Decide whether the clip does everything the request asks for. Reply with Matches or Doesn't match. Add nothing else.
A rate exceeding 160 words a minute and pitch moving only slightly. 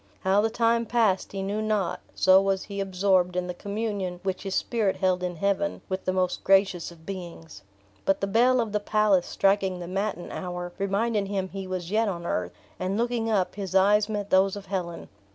Matches